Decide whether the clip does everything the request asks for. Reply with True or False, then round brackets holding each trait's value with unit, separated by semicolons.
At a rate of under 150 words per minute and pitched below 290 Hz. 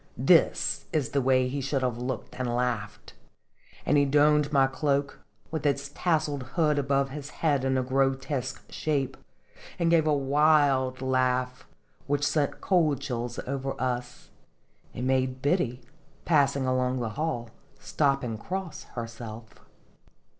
True (140 wpm; 135 Hz)